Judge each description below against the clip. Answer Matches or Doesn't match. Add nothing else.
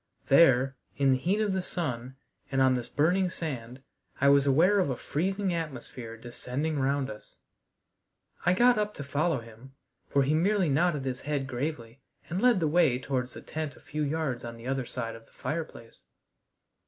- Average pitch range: Matches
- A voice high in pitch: Doesn't match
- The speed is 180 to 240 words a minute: Matches